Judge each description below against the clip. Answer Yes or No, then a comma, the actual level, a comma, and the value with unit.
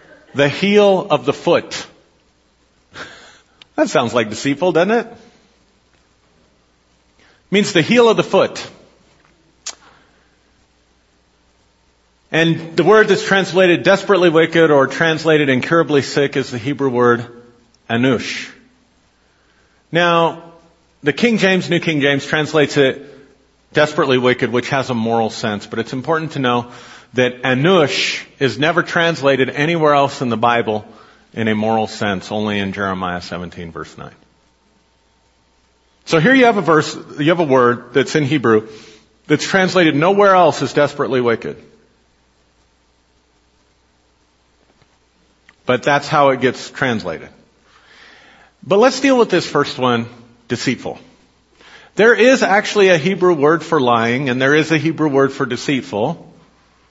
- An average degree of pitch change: No, wide, 7.1 semitones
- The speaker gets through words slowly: Yes, slow, 130 wpm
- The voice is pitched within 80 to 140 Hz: Yes, low, 135 Hz